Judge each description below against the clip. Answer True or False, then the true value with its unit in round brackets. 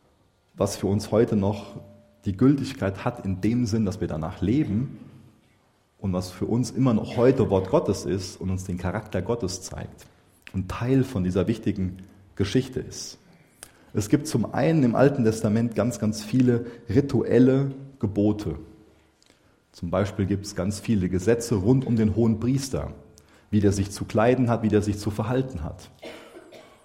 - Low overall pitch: True (110 Hz)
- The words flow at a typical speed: True (165 wpm)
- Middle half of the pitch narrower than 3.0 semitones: False (3.5 semitones)